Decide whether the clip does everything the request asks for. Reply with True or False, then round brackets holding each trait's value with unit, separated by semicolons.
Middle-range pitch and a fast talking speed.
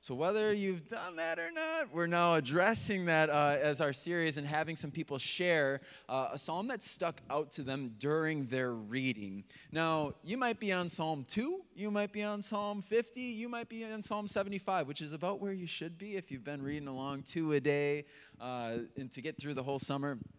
True (160 Hz; 215 wpm)